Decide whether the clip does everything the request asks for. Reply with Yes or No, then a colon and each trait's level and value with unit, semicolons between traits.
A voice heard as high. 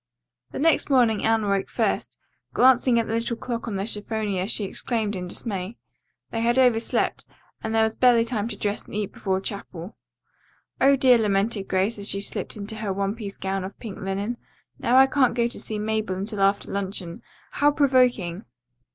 Yes: high, 215 Hz